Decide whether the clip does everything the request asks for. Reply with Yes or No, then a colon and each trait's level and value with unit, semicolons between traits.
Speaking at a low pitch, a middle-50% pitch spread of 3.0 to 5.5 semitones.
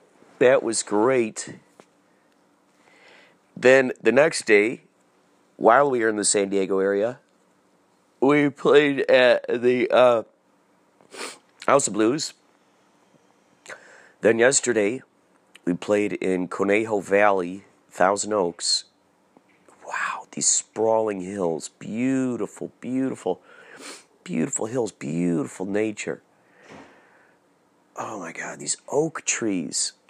Yes: low, 105 Hz; average, 4.2 semitones